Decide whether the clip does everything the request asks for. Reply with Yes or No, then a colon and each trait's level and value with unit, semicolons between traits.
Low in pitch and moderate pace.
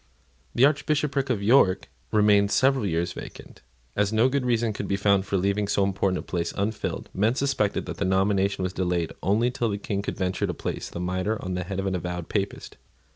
No: low, 100 Hz; fast, 210 wpm